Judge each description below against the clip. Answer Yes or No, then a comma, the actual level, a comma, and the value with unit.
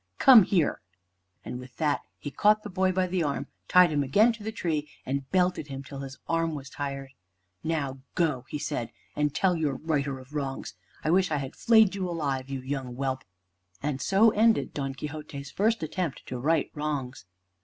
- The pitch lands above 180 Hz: No, medium, 150 Hz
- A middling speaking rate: Yes, average, 190 wpm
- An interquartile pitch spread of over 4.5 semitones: Yes, average, 5.0 semitones